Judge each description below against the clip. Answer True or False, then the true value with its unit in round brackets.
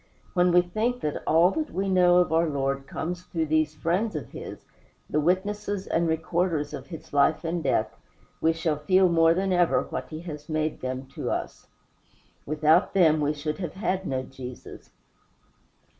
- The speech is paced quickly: False (175 wpm)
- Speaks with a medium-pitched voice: True (165 Hz)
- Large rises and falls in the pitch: False (3.1 semitones)